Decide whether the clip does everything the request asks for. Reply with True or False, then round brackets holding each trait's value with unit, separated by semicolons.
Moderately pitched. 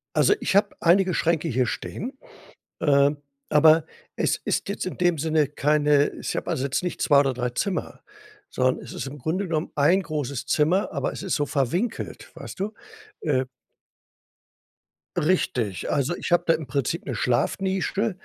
True (155 Hz)